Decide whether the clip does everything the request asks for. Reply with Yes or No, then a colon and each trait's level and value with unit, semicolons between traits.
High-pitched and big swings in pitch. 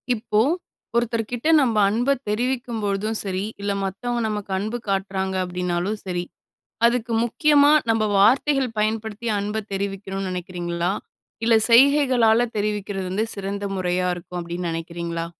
No: high, 205 Hz; average, 3.7 semitones